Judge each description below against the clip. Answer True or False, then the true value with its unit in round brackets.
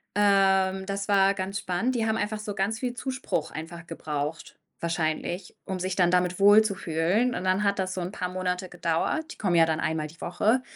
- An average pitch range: True (3.0 semitones)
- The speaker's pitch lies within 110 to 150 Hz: False (190 Hz)